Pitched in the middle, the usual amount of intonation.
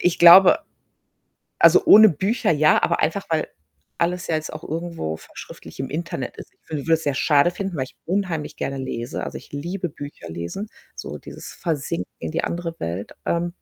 Yes: medium, 160 Hz; average, 4.1 semitones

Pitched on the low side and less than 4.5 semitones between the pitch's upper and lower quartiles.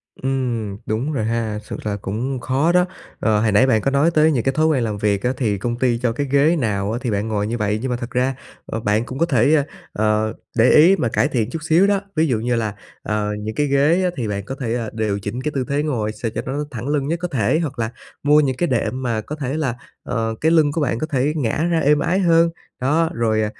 No: low, 125 Hz; average, 5.2 semitones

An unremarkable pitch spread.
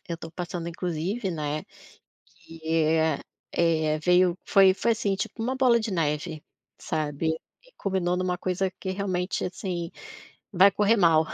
Yes: average, 3.1 semitones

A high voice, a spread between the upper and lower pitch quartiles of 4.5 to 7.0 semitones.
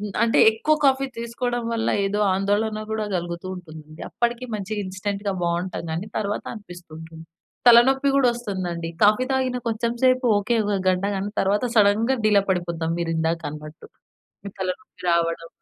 Yes: high, 200 Hz; average, 5.2 semitones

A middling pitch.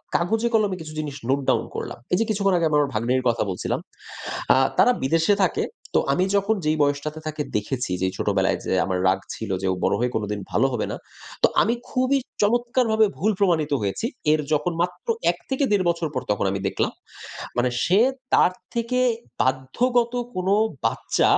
Yes: medium, 160 Hz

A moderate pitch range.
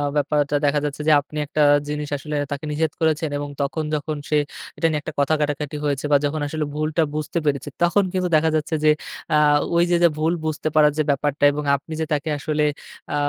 No: narrow, 1.4 semitones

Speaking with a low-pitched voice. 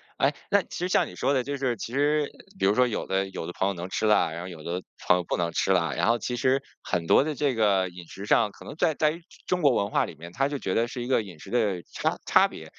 Yes: low, 110 Hz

